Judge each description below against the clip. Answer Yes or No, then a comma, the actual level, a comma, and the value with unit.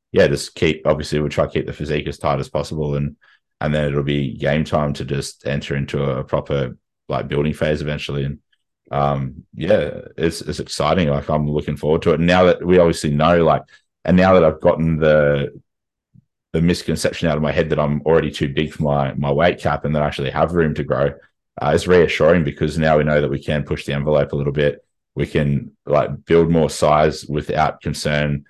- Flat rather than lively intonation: Yes, narrow, 1.5 semitones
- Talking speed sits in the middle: No, fast, 220 wpm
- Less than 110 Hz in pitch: Yes, very low, 75 Hz